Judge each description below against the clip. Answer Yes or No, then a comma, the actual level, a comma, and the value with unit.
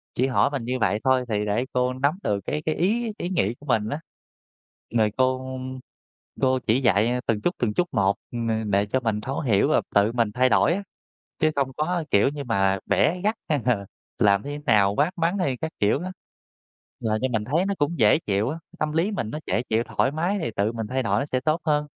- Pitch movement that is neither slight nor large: No, wide, 6.0 semitones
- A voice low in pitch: Yes, low, 130 Hz